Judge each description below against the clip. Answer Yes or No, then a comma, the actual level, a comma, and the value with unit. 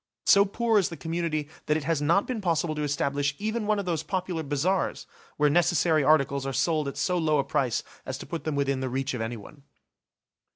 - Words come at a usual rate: No, fast, 215 wpm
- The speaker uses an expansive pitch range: No, average, 4.0 semitones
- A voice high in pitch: No, medium, 155 Hz